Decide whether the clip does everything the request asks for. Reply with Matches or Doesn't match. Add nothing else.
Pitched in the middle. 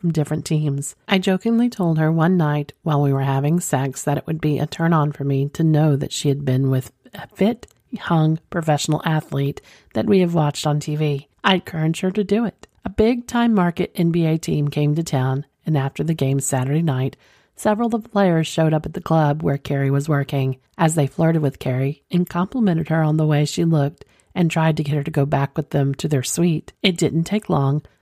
Matches